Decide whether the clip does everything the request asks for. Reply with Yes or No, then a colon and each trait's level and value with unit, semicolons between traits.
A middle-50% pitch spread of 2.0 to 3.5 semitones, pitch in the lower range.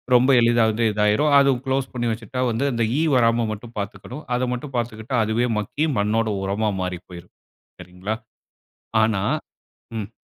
Yes: average, 2.8 semitones; low, 115 Hz